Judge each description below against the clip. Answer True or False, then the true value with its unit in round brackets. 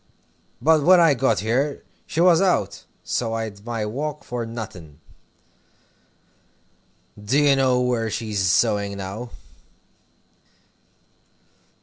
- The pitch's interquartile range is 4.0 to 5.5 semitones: True (5.1 semitones)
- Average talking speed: False (105 wpm)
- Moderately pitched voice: False (120 Hz)